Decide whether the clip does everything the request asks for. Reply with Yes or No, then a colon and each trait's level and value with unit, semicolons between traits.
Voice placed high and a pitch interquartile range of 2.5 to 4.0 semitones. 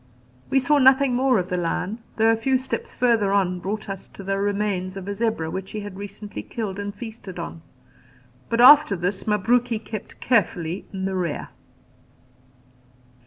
Yes: high, 205 Hz; average, 3.6 semitones